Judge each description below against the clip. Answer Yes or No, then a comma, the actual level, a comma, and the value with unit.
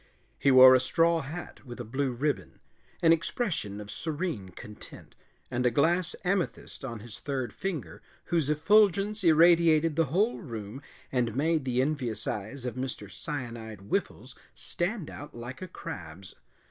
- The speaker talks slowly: No, average, 150 wpm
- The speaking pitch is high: No, medium, 140 Hz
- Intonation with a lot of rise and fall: Yes, wide, 5.7 semitones